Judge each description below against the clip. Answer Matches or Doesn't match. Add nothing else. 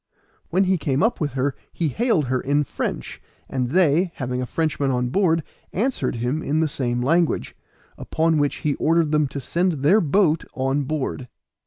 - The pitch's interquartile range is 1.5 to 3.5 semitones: Doesn't match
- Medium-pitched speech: Matches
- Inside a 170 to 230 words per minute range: Matches